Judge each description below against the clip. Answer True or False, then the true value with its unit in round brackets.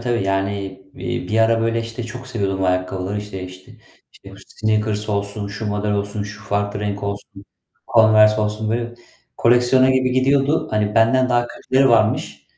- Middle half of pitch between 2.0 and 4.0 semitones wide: True (2.5 semitones)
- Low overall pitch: True (110 Hz)